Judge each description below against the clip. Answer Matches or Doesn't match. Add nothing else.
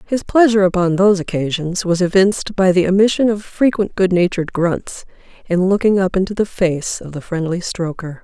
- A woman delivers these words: Matches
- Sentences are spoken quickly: Doesn't match